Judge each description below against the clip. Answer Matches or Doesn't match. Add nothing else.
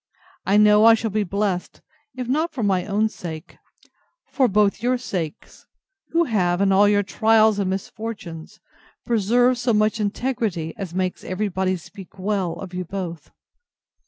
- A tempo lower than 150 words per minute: Doesn't match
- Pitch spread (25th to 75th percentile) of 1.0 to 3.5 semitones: Matches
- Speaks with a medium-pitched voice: Doesn't match